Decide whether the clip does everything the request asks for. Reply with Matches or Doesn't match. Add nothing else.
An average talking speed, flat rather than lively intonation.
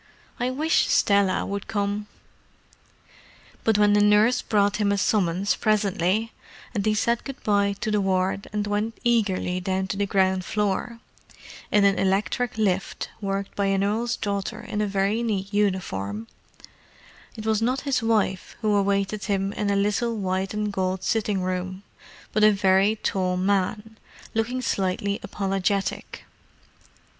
Matches